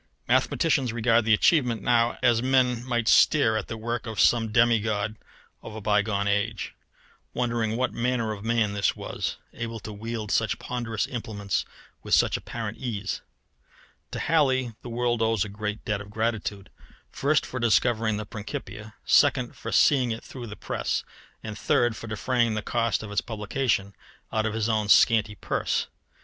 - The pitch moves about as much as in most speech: No, narrow, 2.2 semitones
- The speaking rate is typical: Yes, average, 165 wpm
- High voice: No, low, 115 Hz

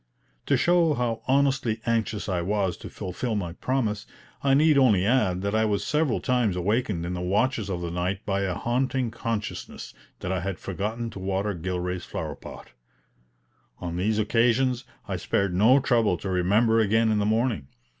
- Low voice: Yes, low, 105 Hz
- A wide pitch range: No, average, 4.5 semitones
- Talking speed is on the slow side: No, average, 175 wpm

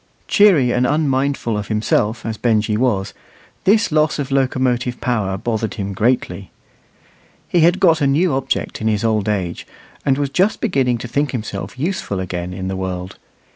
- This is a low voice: Yes, low, 120 Hz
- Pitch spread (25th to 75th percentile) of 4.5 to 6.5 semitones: Yes, average, 5.2 semitones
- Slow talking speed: No, average, 170 wpm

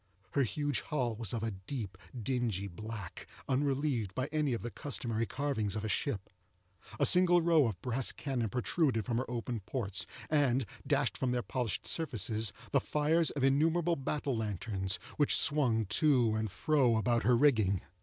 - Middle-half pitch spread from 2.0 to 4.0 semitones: No, average, 4.8 semitones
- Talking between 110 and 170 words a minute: Yes, average, 165 wpm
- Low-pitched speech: Yes, low, 125 Hz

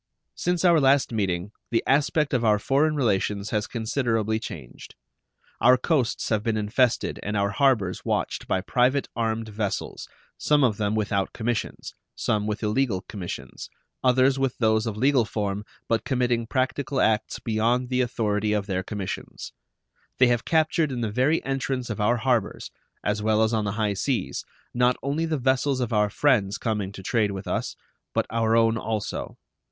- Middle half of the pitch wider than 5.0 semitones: No, average, 3.6 semitones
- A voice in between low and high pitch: No, low, 115 Hz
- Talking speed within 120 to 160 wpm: No, average, 170 wpm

